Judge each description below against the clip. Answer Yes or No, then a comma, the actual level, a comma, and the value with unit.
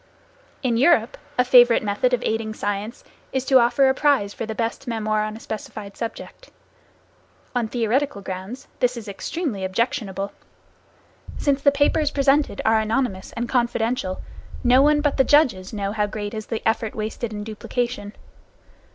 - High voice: Yes, high, 230 Hz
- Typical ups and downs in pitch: Yes, average, 3.7 semitones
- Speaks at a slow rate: No, average, 160 wpm